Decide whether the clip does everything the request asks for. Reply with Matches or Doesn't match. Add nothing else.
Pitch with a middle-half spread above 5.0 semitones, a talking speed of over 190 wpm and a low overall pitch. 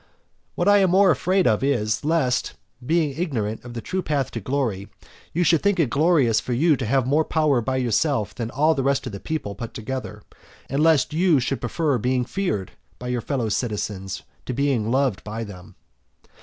Matches